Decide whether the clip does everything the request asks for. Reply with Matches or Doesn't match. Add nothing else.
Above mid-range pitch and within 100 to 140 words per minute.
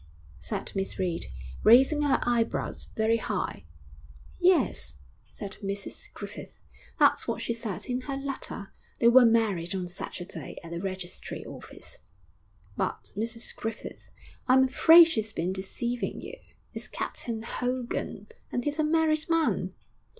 Matches